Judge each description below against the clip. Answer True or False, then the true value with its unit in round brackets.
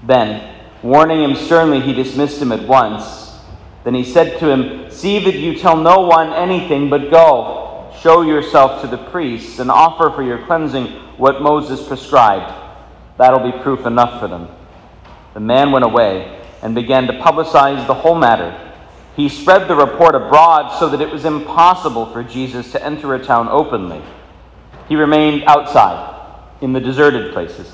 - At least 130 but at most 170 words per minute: True (165 wpm)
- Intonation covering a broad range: False (4.0 semitones)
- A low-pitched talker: False (145 Hz)